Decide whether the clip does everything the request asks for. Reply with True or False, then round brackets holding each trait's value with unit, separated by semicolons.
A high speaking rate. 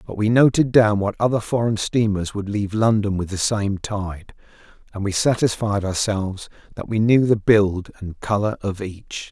False (180 wpm)